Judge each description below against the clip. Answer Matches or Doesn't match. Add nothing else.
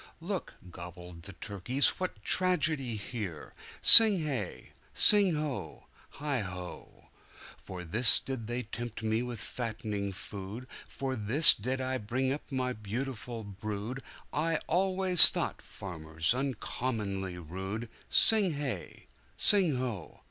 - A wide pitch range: Matches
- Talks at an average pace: Doesn't match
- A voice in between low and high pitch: Doesn't match